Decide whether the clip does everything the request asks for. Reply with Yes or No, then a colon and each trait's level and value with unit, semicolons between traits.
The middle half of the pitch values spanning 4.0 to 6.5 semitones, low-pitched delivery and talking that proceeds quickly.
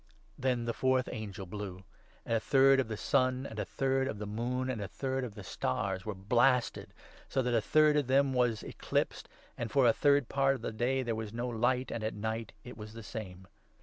No: average, 3.4 semitones; low, 120 Hz; fast, 230 wpm